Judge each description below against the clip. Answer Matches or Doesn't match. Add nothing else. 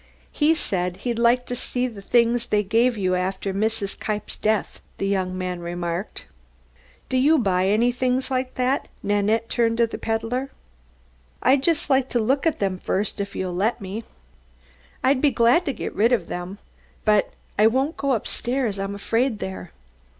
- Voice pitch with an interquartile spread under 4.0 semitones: Doesn't match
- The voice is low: Doesn't match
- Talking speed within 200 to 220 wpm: Doesn't match